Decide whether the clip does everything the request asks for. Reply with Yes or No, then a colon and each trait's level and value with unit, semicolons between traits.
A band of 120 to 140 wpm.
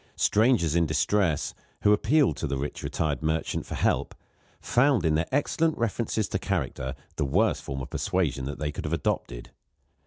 No: average, 175 wpm